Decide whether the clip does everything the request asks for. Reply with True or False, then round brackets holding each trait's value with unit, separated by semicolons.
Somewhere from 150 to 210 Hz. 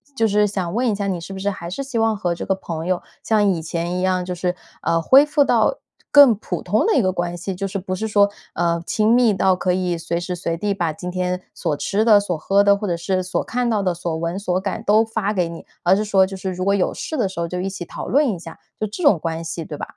True (190 Hz)